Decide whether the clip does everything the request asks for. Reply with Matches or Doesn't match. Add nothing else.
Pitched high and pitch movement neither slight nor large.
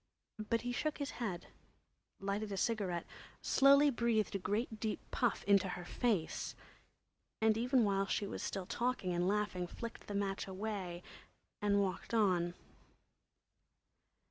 Matches